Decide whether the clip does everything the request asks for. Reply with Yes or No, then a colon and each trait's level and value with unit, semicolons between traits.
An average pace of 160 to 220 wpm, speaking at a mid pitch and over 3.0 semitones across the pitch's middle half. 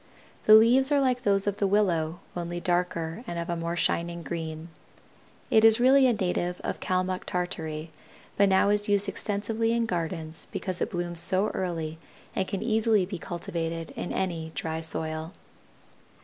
Yes: average, 165 wpm; medium, 180 Hz; average, 3.7 semitones